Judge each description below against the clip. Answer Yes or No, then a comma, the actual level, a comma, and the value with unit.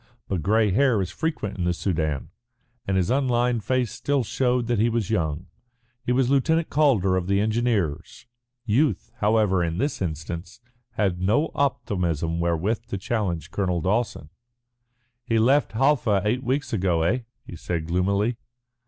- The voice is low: Yes, low, 105 Hz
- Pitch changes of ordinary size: No, wide, 5.7 semitones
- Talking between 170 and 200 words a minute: No, average, 155 wpm